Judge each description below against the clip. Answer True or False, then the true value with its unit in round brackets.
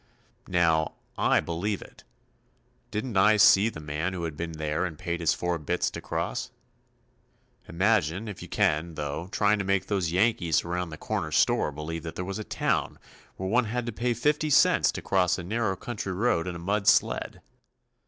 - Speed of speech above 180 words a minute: True (190 wpm)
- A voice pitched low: True (90 Hz)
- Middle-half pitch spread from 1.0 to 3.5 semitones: False (4.2 semitones)